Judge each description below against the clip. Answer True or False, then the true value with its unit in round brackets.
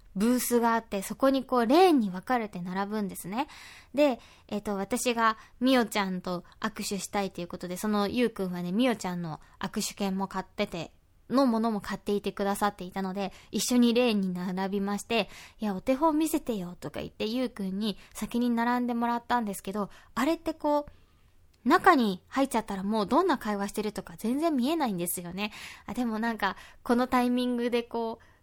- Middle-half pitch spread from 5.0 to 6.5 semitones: False (4.0 semitones)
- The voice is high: True (215 Hz)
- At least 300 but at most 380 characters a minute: False (395 characters per minute)